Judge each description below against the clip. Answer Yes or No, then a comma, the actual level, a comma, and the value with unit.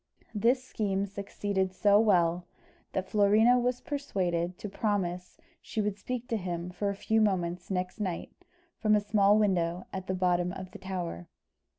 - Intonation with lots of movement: No, average, 2.8 semitones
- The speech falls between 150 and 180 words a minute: Yes, average, 165 wpm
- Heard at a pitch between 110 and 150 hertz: No, high, 195 Hz